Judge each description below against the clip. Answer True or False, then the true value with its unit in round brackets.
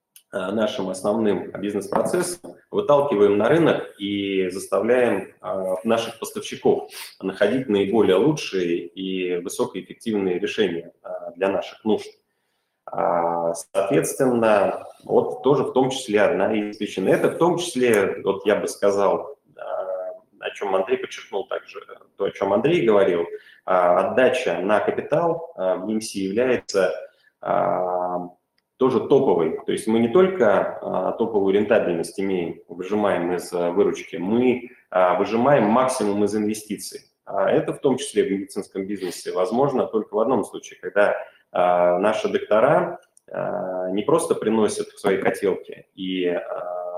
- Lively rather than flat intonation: True (7.6 semitones)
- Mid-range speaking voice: False (105 Hz)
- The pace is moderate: True (135 wpm)